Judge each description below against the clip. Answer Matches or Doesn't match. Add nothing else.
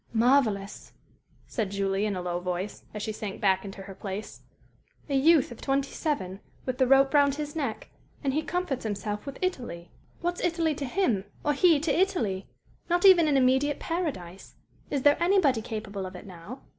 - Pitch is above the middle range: Matches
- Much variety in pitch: Matches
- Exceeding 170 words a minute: Matches